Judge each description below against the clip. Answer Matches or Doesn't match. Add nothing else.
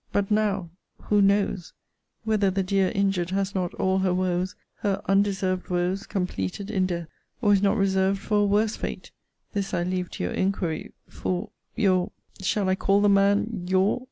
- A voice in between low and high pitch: Doesn't match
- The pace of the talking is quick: Doesn't match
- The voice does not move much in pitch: Matches